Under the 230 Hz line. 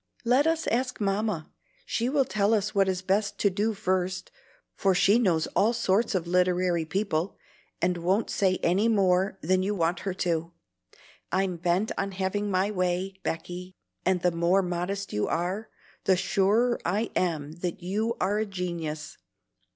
Yes: high, 190 Hz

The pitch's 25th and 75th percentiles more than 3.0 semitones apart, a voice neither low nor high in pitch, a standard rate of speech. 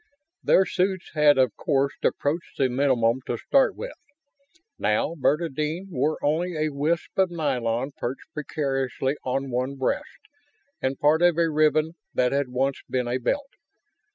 Yes: average, 3.7 semitones; medium, 145 Hz; average, 150 wpm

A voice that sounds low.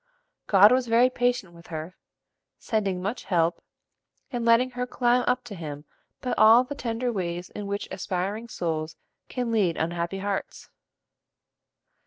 No: high, 205 Hz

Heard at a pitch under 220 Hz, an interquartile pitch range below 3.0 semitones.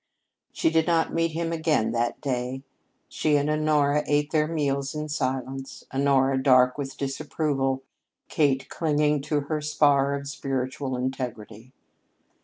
Yes: medium, 140 Hz; narrow, 2.4 semitones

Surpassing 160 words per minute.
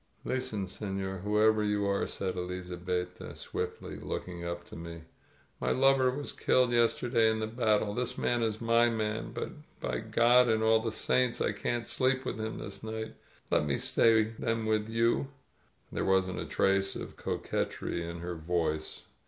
Yes: average, 170 wpm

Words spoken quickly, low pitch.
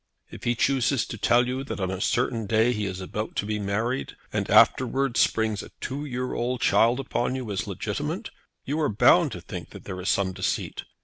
Yes: fast, 210 wpm; low, 115 Hz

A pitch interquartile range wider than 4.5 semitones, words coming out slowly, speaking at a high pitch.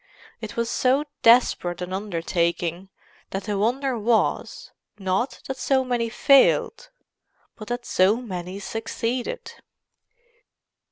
Yes: average, 4.9 semitones; slow, 110 wpm; high, 225 Hz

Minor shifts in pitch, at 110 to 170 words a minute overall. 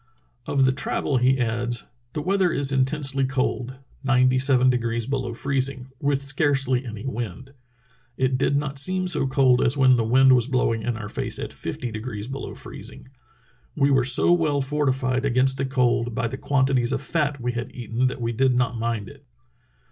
No: narrow, 2.1 semitones; average, 185 wpm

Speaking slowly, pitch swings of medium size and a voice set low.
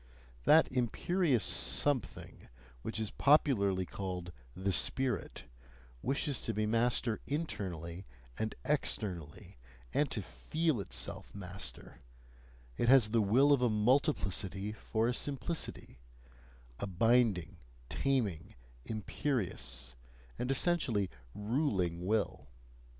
No: slow, 100 wpm; wide, 5.8 semitones; low, 110 Hz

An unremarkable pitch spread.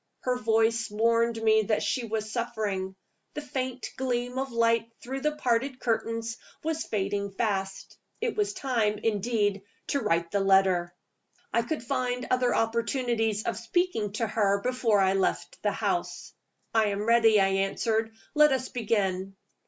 Yes: average, 3.4 semitones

